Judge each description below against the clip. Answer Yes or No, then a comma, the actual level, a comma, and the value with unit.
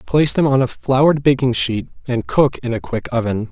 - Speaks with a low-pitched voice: Yes, low, 130 Hz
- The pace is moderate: No, fast, 220 wpm